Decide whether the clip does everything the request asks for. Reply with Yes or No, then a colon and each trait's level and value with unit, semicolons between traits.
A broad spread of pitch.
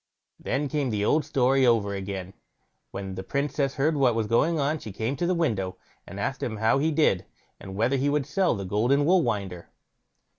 Yes: wide, 6.2 semitones